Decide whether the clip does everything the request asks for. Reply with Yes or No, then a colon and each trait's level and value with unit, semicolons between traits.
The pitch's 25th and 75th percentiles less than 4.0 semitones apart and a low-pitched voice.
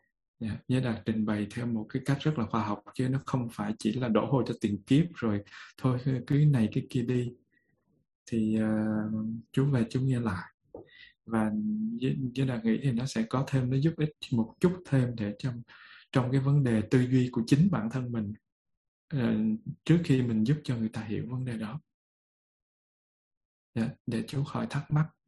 Yes: average, 3.5 semitones; low, 120 Hz